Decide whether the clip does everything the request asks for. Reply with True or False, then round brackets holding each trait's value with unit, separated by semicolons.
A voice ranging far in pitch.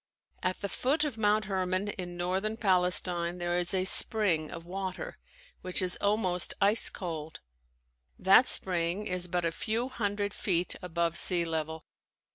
False (2.8 semitones)